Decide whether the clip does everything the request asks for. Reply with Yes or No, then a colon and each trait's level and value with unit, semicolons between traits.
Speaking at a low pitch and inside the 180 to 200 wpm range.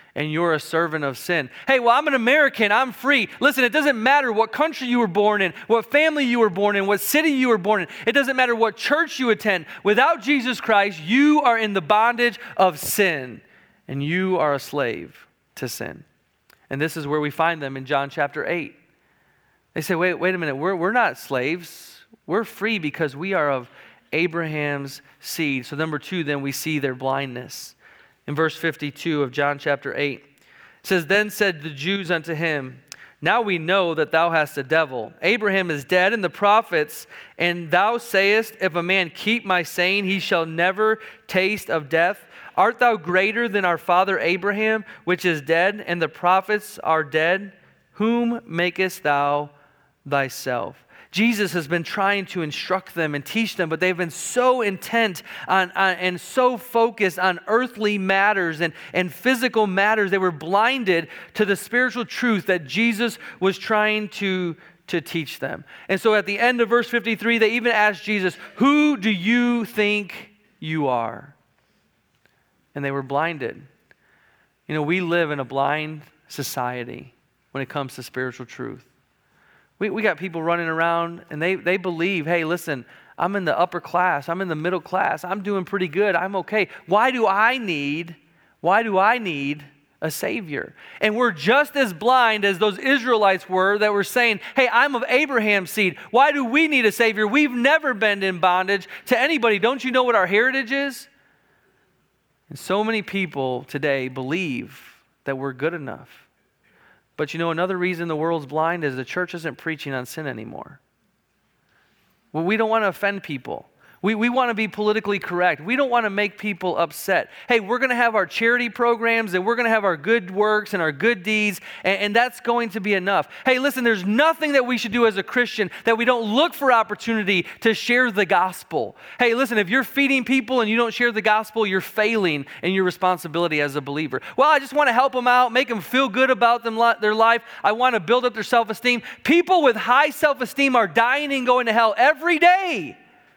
No: high, 195 Hz; average, 195 wpm